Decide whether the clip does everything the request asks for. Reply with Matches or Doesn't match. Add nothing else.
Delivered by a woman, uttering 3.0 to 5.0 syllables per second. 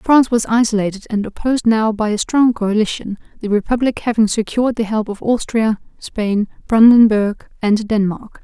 Doesn't match